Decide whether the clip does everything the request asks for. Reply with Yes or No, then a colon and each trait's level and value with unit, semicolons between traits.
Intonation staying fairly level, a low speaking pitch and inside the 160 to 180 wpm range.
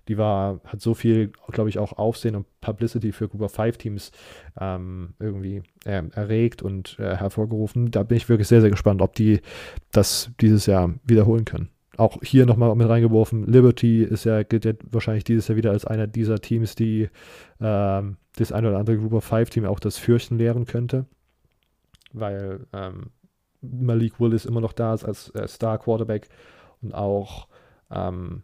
Yes: narrow, 2.2 semitones; low, 110 Hz; average, 175 wpm